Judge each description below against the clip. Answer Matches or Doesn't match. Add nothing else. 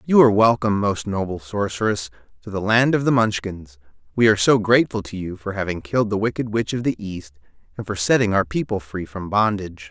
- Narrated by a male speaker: Matches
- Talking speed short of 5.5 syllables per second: Doesn't match